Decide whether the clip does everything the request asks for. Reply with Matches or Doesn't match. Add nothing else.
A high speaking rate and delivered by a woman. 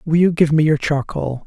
Doesn't match